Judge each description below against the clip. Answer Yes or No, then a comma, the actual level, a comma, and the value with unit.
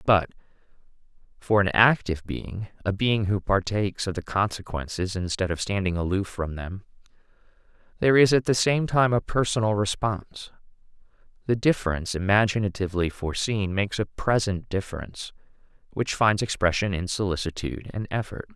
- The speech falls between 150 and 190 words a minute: No, slow, 135 wpm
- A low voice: Yes, low, 100 Hz